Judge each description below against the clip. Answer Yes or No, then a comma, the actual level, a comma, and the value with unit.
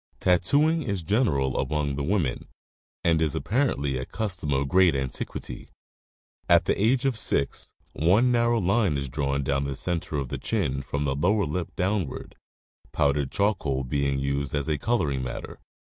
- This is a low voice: Yes, very low, 75 Hz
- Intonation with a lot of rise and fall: Yes, wide, 6.6 semitones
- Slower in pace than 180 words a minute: Yes, average, 160 wpm